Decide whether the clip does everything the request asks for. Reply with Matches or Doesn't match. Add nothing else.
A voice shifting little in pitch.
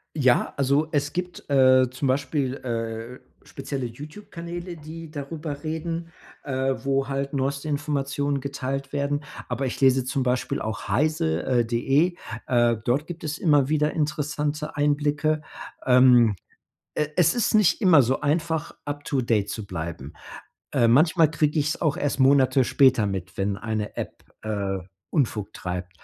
Doesn't match